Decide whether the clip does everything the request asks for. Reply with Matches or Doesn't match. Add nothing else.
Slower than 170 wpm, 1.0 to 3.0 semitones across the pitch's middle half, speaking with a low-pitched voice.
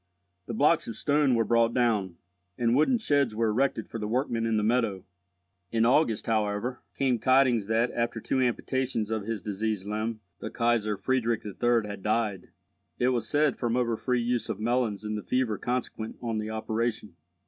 Doesn't match